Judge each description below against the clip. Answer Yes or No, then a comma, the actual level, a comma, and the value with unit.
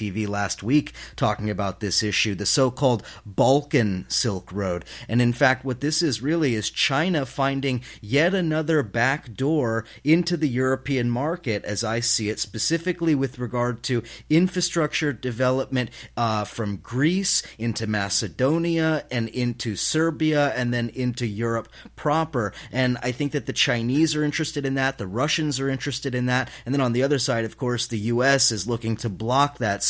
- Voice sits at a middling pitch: No, low, 125 Hz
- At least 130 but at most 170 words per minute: Yes, average, 165 wpm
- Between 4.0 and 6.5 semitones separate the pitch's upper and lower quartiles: Yes, average, 4.3 semitones